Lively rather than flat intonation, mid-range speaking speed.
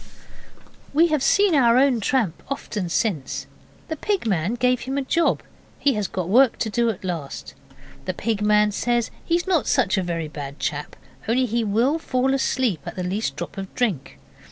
Yes: wide, 6.0 semitones; average, 190 wpm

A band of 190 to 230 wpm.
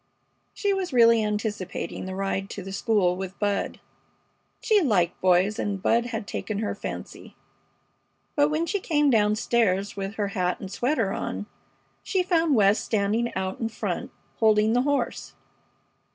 No: average, 155 wpm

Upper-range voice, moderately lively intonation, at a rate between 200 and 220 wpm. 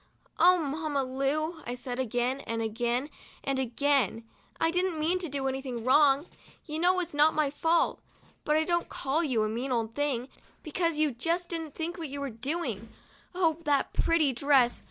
No: very high, 285 Hz; average, 4.2 semitones; average, 185 wpm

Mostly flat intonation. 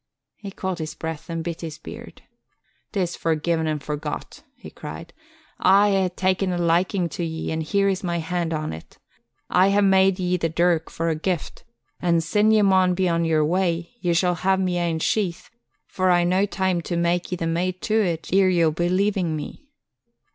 Yes: narrow, 2.3 semitones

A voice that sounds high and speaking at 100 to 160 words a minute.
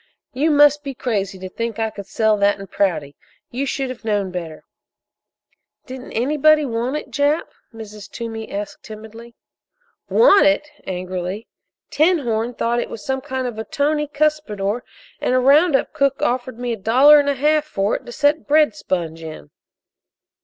No: high, 240 Hz; average, 170 wpm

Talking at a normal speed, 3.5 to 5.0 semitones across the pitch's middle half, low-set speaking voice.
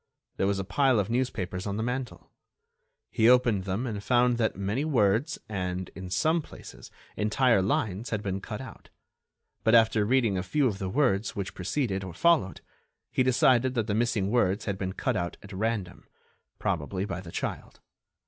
Yes: average, 175 wpm; average, 4.4 semitones; low, 105 Hz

